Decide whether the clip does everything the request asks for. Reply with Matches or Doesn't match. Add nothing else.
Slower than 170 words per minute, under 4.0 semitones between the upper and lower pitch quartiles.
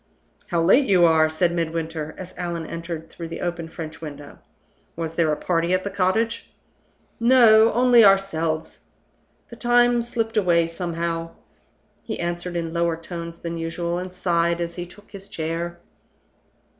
Matches